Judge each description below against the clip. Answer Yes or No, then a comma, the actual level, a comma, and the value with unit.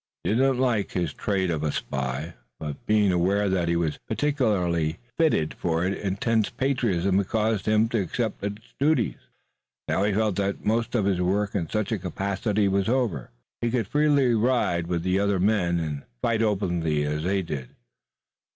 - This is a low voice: Yes, low, 100 Hz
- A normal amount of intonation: Yes, average, 4.4 semitones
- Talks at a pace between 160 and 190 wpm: Yes, average, 180 wpm